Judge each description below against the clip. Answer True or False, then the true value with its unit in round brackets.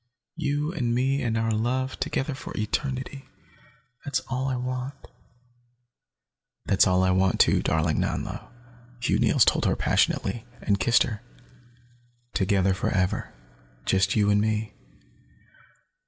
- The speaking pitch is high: False (115 Hz)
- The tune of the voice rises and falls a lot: False (5.0 semitones)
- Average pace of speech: False (125 wpm)